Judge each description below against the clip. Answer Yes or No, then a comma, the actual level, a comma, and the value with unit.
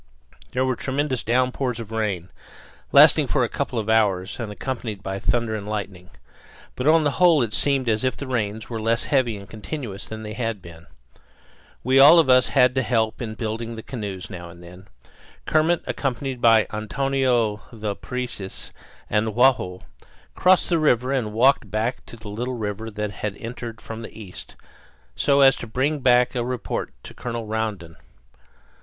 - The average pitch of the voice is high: No, low, 115 Hz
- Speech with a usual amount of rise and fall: Yes, average, 3.4 semitones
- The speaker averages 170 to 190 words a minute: Yes, average, 180 wpm